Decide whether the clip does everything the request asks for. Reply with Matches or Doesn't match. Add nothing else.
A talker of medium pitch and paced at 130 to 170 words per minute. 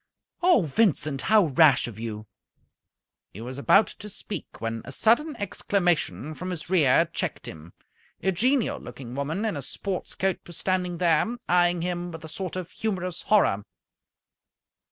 Matches